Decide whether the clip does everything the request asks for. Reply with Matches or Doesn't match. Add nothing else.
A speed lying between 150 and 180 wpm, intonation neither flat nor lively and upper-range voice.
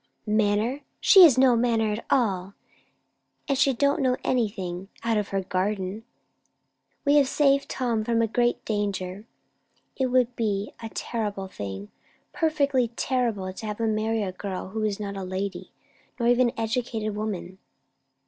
Matches